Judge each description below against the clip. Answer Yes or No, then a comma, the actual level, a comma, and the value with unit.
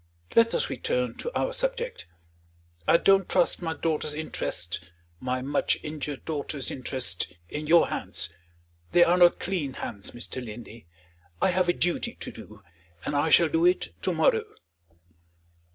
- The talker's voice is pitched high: No, medium, 155 Hz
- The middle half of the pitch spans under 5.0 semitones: No, wide, 5.5 semitones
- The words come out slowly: No, average, 150 wpm